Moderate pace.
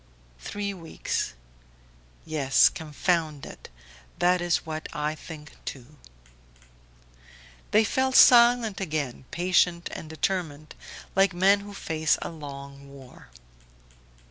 No: slow, 105 wpm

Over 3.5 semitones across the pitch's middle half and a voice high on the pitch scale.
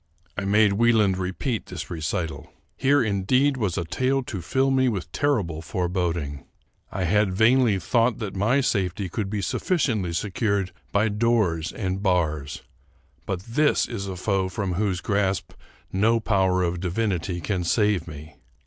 No: average, 3.9 semitones; low, 100 Hz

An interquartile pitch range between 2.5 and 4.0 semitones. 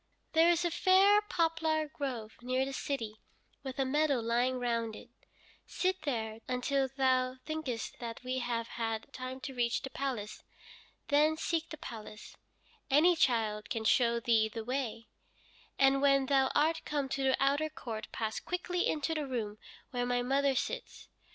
No: average, 4.5 semitones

